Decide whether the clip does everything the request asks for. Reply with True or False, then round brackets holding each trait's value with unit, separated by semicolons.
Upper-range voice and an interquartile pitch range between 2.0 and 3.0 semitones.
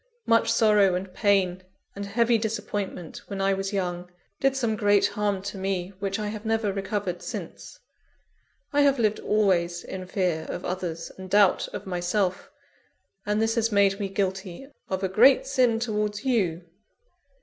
True (200 Hz; 2.7 semitones)